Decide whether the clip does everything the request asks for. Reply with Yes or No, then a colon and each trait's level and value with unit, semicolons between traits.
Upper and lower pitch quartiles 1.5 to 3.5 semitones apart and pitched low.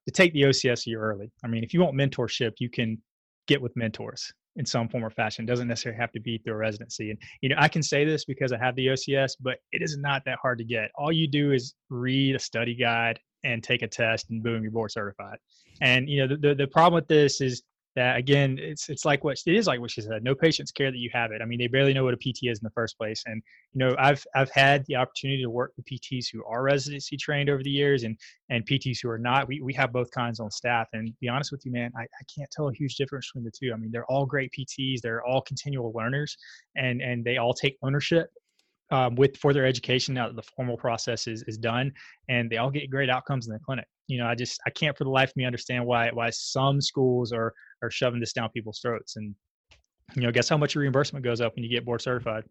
Yes: average, 2.8 semitones; low, 125 Hz